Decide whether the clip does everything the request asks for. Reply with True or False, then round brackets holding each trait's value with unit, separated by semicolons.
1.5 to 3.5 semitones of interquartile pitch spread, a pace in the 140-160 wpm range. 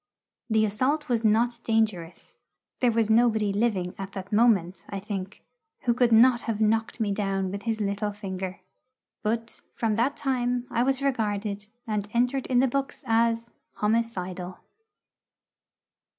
True (2.9 semitones; 145 wpm)